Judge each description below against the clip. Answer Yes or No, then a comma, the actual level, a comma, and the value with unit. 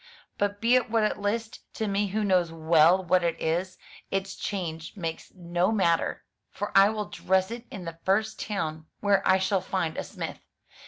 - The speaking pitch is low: No, high, 190 Hz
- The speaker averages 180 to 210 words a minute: Yes, average, 190 wpm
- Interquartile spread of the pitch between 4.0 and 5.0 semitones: No, average, 3.3 semitones